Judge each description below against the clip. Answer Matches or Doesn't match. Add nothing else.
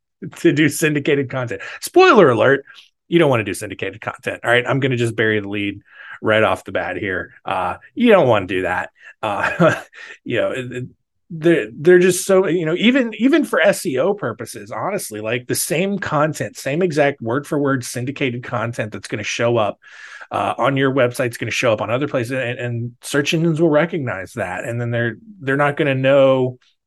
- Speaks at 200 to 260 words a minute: Matches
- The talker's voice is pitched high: Doesn't match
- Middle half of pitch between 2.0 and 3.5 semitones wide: Doesn't match